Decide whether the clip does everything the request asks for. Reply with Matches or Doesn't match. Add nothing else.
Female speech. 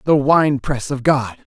Doesn't match